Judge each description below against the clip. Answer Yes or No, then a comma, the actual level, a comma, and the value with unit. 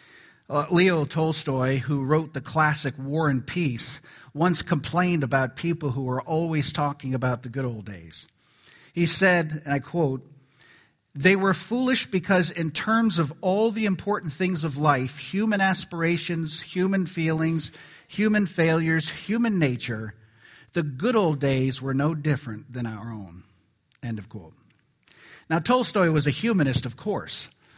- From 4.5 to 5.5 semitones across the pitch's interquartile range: Yes, average, 5.0 semitones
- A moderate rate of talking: Yes, average, 150 wpm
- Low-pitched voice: No, medium, 155 Hz